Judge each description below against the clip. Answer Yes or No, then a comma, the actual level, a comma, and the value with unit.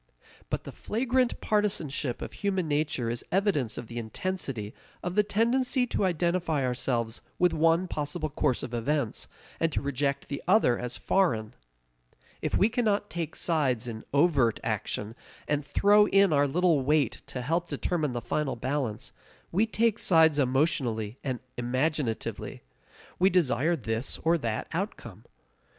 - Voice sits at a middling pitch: Yes, medium, 150 Hz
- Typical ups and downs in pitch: No, wide, 6.6 semitones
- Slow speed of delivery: No, average, 145 wpm